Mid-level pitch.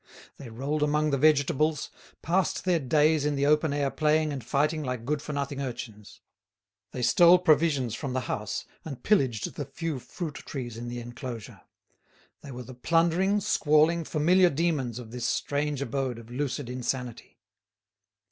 Yes: medium, 145 Hz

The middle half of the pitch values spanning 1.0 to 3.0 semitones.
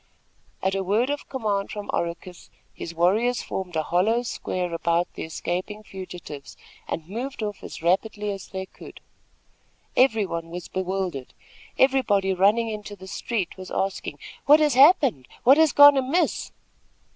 No: average, 5.1 semitones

